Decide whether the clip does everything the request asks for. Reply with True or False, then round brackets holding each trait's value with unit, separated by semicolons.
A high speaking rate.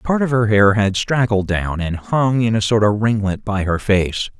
True (230 wpm)